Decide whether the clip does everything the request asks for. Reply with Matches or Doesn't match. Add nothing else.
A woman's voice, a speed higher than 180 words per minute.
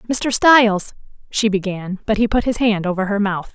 Matches